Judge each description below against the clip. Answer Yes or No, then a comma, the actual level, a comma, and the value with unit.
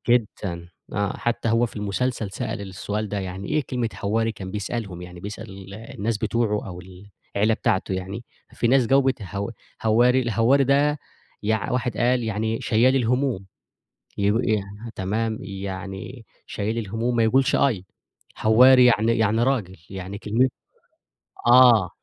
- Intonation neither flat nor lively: Yes, average, 3.4 semitones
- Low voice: Yes, low, 110 Hz